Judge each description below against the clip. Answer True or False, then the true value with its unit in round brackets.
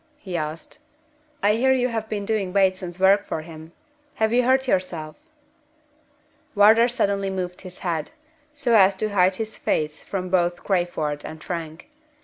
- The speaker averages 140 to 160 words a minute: True (155 wpm)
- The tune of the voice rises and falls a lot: False (3.9 semitones)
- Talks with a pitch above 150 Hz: True (190 Hz)